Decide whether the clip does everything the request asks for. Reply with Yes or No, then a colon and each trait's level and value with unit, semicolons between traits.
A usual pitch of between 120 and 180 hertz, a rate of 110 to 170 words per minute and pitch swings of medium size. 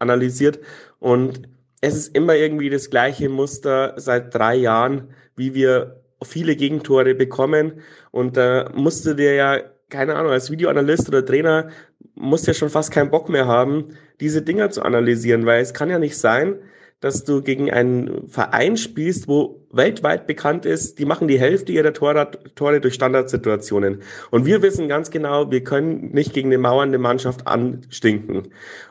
Yes: low, 135 Hz; average, 165 wpm; average, 3.3 semitones